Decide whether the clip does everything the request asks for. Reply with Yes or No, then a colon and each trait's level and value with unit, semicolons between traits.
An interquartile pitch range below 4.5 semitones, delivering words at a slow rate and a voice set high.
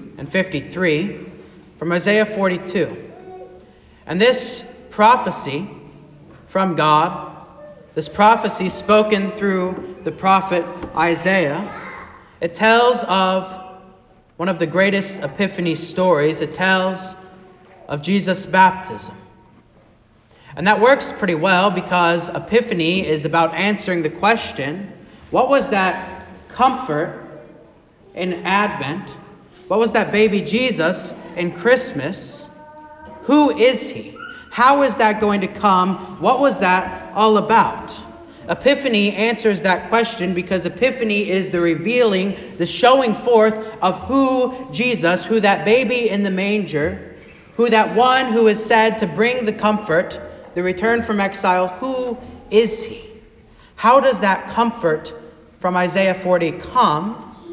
Yes: average, 4.1 semitones; slow, 120 wpm; high, 195 Hz